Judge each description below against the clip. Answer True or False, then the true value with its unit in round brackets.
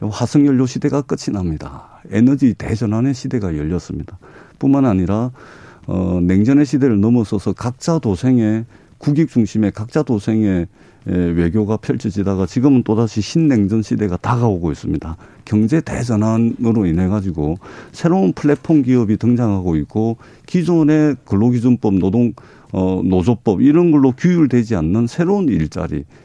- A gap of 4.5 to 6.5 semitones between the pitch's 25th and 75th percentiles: True (5.1 semitones)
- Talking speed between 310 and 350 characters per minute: True (325 characters per minute)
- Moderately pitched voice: False (115 Hz)